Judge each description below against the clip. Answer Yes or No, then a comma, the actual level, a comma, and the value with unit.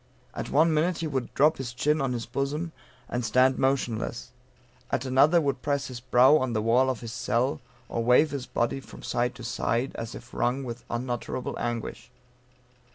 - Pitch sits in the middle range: No, low, 130 Hz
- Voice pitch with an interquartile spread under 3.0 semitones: Yes, narrow, 2.6 semitones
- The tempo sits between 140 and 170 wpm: No, average, 185 wpm